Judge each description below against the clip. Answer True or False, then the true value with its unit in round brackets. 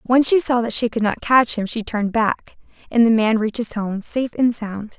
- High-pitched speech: True (225 Hz)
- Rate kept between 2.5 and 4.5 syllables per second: False (5.3 syllables/s)